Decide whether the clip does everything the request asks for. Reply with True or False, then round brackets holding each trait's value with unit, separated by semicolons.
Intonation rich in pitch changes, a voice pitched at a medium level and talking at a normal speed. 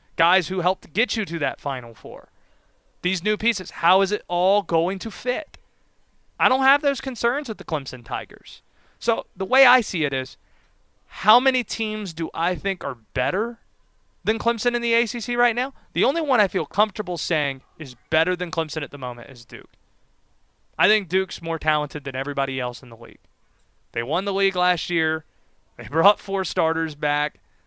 True (6.5 semitones; 180 Hz; 190 wpm)